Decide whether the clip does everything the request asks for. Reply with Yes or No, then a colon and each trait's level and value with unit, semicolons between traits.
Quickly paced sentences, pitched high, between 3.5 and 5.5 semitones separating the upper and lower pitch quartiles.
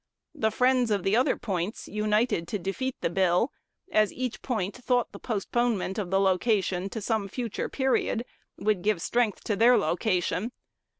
No: average, 165 wpm; high, 215 Hz; average, 3.8 semitones